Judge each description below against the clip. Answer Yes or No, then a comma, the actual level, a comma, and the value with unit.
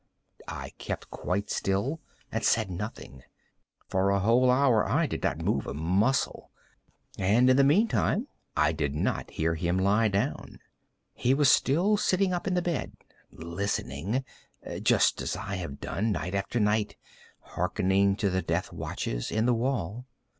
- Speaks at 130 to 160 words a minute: Yes, average, 155 wpm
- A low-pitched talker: Yes, low, 105 Hz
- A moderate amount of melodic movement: No, wide, 5.7 semitones